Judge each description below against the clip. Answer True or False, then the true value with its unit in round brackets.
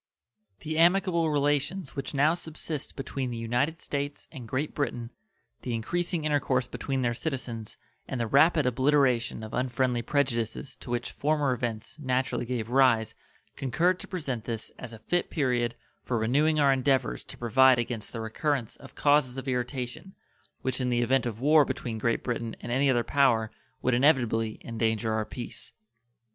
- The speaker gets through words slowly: False (165 wpm)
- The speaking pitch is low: True (130 Hz)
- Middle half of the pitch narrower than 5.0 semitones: True (3.6 semitones)